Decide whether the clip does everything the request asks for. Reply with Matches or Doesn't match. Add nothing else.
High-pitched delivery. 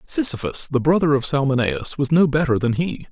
Doesn't match